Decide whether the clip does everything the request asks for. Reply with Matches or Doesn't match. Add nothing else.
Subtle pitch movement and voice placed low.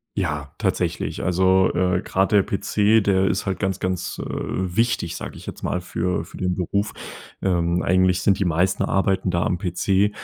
Matches